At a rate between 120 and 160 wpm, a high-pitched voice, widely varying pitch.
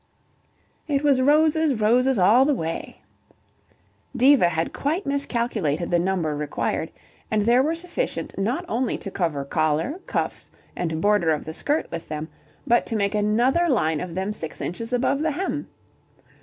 Yes: average, 155 wpm; high, 220 Hz; wide, 8.5 semitones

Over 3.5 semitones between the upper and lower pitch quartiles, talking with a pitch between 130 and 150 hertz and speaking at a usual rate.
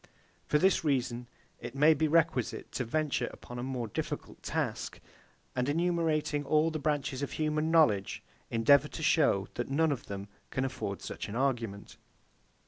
Yes: average, 4.3 semitones; medium, 140 Hz; average, 160 wpm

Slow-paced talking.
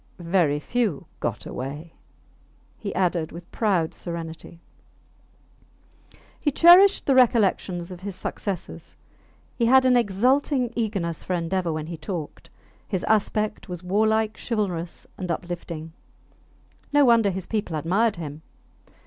Yes: slow, 125 wpm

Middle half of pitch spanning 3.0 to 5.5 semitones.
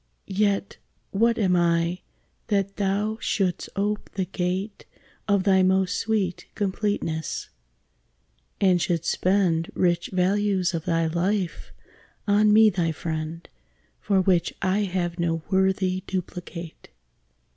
No: narrow, 2.6 semitones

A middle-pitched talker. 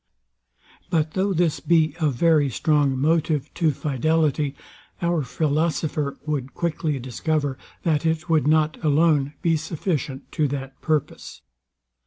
Yes: medium, 155 Hz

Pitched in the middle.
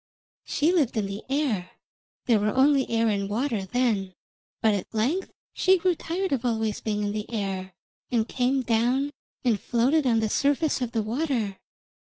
No: high, 235 Hz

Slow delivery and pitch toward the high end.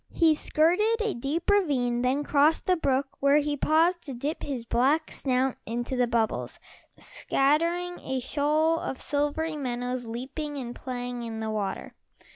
No: average, 155 wpm; very high, 280 Hz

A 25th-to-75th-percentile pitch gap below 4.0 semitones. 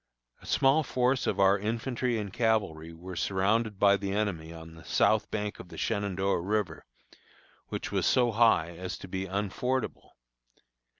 Yes: average, 3.4 semitones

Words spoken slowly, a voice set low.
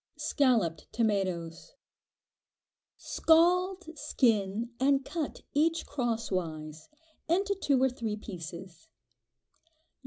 No: slow, 80 wpm; high, 235 Hz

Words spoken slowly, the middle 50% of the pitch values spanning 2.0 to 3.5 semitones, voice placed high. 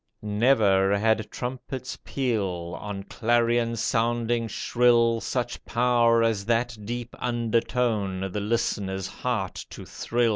No: slow, 110 wpm; narrow, 2.6 semitones; low, 115 Hz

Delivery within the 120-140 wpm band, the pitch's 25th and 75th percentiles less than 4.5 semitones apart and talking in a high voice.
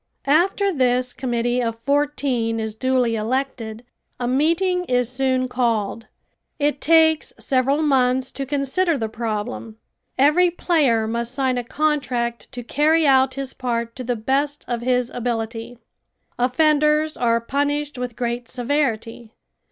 Yes: slow, 135 wpm; average, 3.5 semitones; very high, 255 Hz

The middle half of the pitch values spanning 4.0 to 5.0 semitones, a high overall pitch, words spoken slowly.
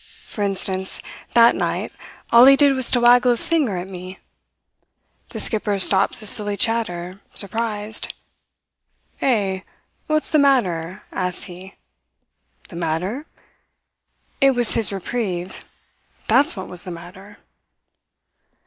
Yes: average, 4.6 semitones; high, 205 Hz; slow, 120 wpm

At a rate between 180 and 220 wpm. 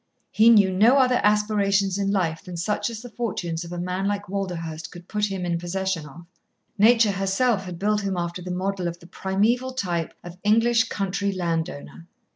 Yes: average, 195 wpm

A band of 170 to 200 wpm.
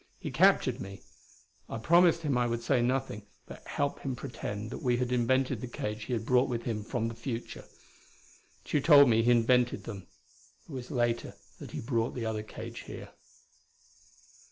Yes: average, 180 wpm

